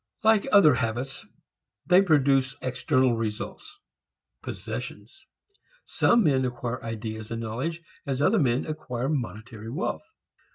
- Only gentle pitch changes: No, average, 5.1 semitones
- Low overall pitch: Yes, low, 130 Hz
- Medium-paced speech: No, slow, 115 wpm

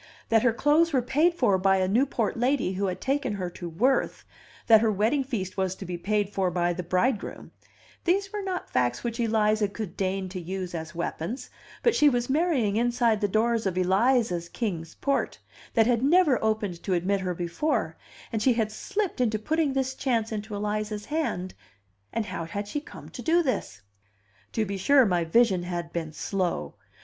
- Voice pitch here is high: Yes, high, 215 Hz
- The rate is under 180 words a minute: No, average, 190 wpm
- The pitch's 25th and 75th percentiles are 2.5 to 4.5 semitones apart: No, wide, 5.5 semitones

